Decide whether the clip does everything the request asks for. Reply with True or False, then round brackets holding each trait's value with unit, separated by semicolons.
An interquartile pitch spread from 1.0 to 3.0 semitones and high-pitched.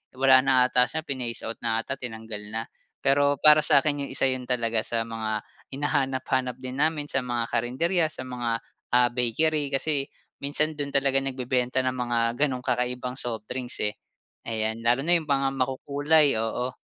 False (2.7 semitones; 130 Hz)